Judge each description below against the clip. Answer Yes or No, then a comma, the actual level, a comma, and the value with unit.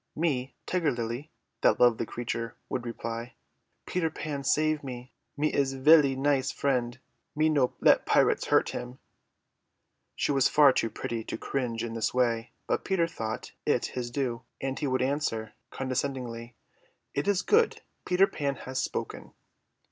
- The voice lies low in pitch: Yes, low, 130 Hz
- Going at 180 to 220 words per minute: No, average, 155 wpm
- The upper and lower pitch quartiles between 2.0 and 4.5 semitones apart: Yes, average, 3.5 semitones